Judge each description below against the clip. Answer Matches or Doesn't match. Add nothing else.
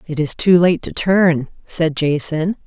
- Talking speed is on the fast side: Doesn't match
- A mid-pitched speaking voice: Matches